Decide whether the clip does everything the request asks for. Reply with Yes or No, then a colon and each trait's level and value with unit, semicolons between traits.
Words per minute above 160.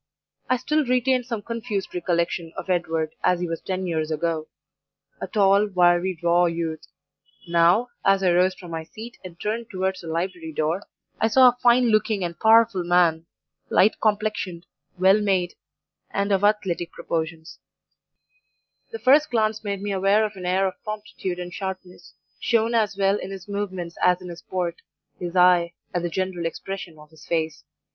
Yes: average, 170 wpm